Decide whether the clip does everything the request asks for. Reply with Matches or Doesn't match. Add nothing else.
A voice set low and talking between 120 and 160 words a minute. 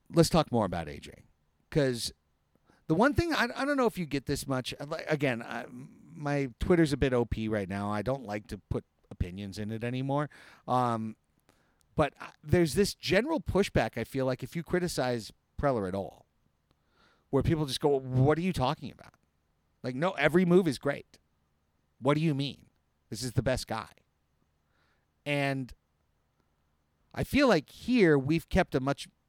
Doesn't match